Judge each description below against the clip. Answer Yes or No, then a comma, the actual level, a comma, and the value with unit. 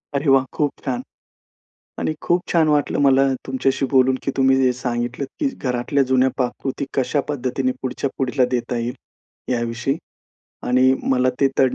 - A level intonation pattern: Yes, narrow, 1.7 semitones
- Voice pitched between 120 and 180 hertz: Yes, low, 130 Hz